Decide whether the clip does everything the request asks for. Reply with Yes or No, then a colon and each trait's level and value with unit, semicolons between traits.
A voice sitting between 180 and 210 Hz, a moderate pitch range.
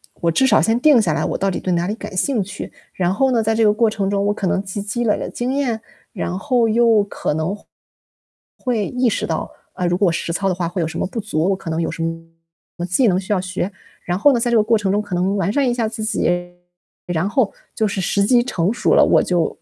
Yes: high, 200 Hz; average, 4.2 semitones